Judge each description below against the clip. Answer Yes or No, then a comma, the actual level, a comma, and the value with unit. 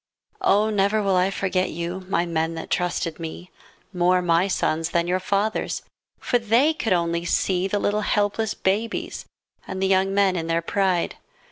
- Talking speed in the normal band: Yes, average, 170 wpm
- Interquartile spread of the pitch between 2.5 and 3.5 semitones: Yes, average, 2.8 semitones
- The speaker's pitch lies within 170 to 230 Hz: Yes, medium, 185 Hz